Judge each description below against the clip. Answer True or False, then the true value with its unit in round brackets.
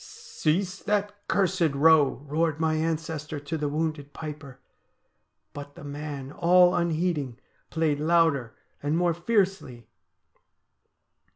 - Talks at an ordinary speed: False (120 wpm)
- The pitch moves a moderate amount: True (3.2 semitones)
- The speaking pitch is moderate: True (160 Hz)